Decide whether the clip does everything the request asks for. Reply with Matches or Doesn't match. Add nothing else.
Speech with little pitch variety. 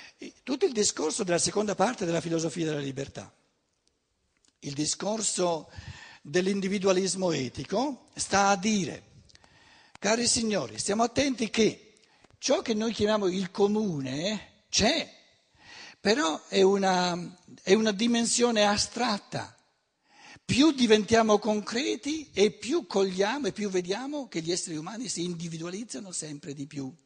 Doesn't match